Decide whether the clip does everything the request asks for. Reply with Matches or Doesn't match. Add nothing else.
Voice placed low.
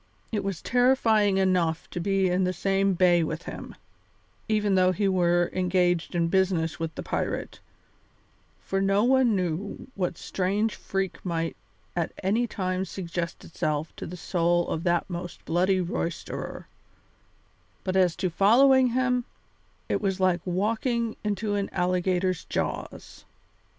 Doesn't match